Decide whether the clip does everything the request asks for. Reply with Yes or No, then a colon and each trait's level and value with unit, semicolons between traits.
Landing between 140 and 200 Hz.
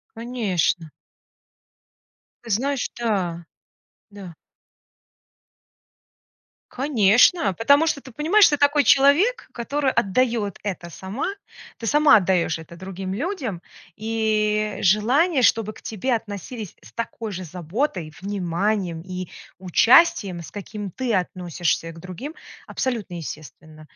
No: high, 210 Hz